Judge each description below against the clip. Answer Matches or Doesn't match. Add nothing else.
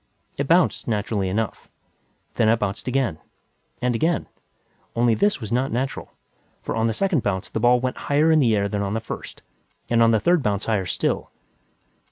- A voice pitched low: Matches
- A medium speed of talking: Matches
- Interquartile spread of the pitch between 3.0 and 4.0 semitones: Doesn't match